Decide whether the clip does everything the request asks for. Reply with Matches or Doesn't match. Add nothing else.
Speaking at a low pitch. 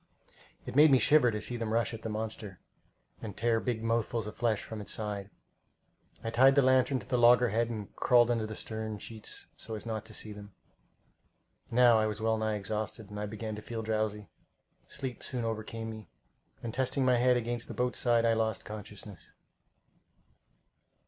Matches